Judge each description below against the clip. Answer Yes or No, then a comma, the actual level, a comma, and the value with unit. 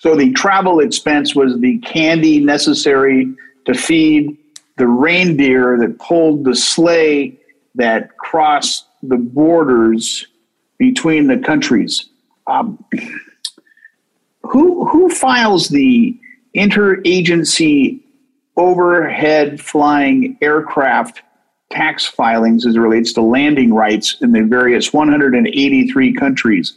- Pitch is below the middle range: No, medium, 175 Hz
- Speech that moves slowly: Yes, slow, 100 wpm